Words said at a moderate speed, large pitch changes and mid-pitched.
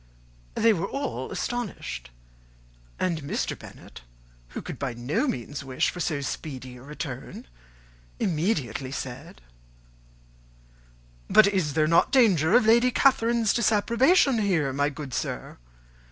No: slow, 125 wpm; wide, 8.5 semitones; medium, 165 Hz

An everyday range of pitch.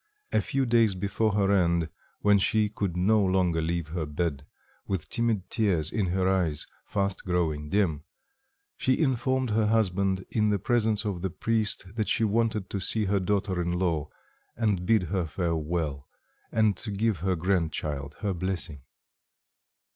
Yes: average, 3.8 semitones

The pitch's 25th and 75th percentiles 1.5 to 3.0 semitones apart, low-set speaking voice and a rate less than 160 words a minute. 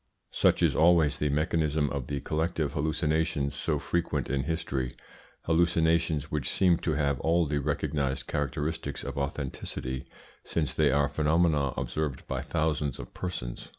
Yes: narrow, 2.5 semitones; very low, 75 Hz; average, 145 wpm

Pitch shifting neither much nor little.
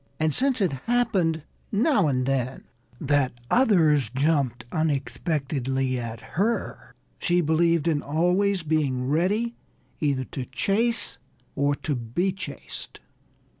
No: wide, 6.1 semitones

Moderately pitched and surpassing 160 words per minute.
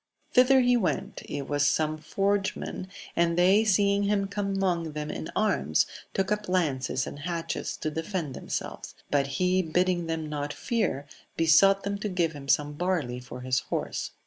Yes: medium, 170 Hz; average, 170 wpm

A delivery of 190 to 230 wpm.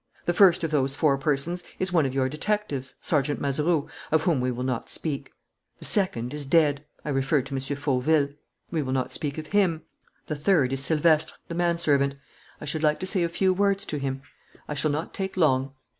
Yes: fast, 205 wpm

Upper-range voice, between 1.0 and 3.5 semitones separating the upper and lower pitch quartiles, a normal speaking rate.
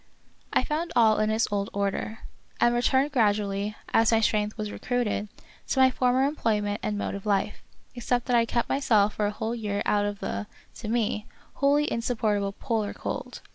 Yes: high, 220 Hz; average, 2.9 semitones; average, 180 wpm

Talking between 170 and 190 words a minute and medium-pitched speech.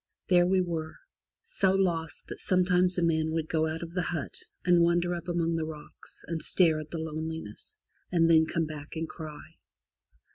Yes: average, 185 wpm; medium, 165 Hz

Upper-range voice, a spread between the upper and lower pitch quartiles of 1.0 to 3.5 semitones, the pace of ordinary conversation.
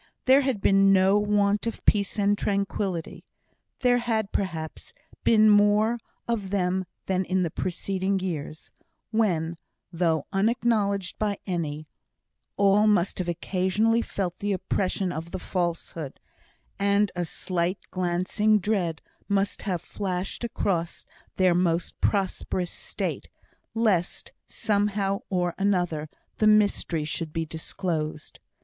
No: high, 195 Hz; average, 2.9 semitones; slow, 120 wpm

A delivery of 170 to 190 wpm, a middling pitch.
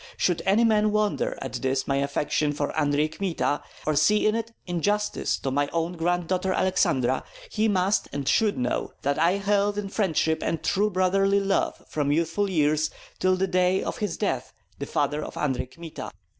Yes: average, 180 wpm; medium, 175 Hz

